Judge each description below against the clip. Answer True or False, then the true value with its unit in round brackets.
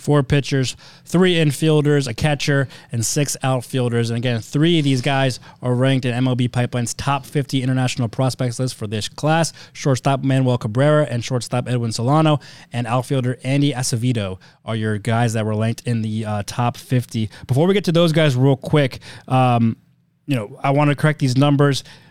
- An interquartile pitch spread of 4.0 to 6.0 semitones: False (3.1 semitones)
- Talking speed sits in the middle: True (180 wpm)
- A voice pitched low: True (130 Hz)